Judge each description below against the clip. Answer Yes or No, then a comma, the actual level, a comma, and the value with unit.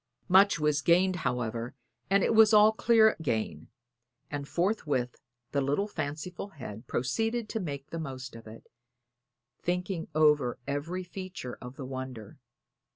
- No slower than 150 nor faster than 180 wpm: No, average, 140 wpm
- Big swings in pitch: Yes, wide, 6.5 semitones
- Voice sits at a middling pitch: Yes, medium, 150 Hz